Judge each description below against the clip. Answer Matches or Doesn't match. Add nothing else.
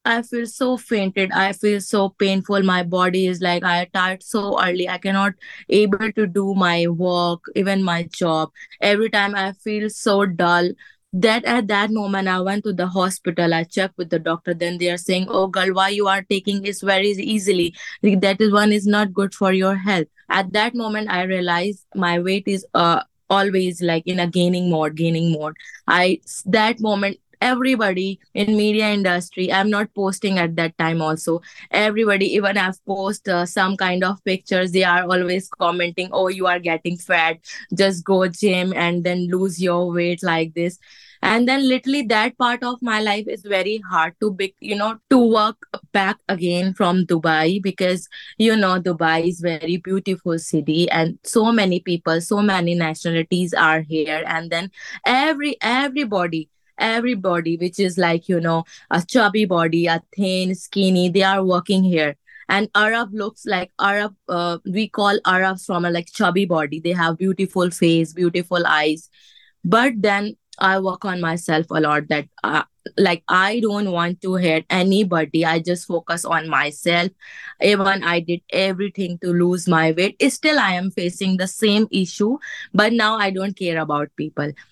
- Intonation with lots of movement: Doesn't match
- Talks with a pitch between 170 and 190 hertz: Matches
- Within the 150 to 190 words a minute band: Matches